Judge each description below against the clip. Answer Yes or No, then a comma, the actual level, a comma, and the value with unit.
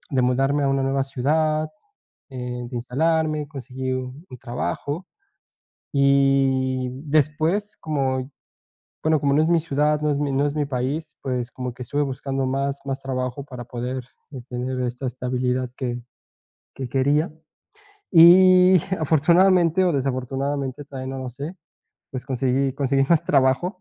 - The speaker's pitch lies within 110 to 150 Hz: Yes, low, 135 Hz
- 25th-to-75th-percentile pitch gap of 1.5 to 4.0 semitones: Yes, average, 2.8 semitones